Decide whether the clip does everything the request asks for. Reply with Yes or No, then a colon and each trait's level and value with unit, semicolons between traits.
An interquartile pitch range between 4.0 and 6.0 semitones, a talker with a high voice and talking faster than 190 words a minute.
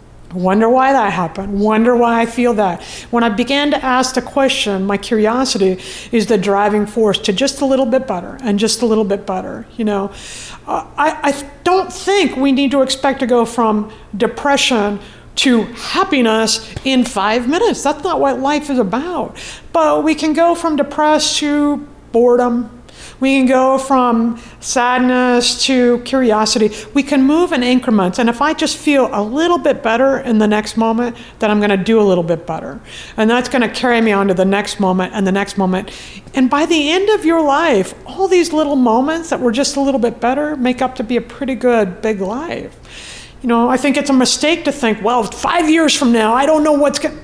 Yes: average, 4.3 semitones; very high, 250 Hz; fast, 205 wpm